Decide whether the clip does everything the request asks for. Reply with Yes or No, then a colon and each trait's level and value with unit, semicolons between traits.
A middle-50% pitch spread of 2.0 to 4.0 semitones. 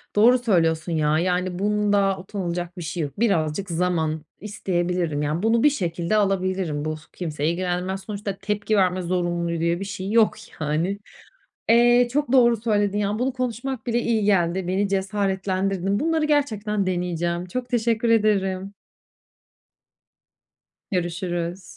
Yes: average, 3.5 semitones